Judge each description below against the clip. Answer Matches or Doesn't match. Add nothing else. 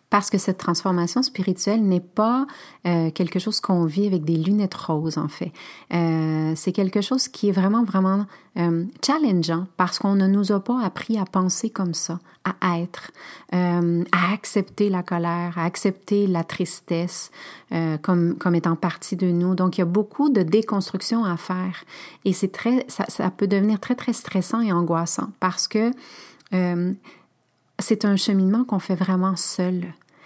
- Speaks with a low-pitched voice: Doesn't match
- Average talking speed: Matches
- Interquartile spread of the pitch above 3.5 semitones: Doesn't match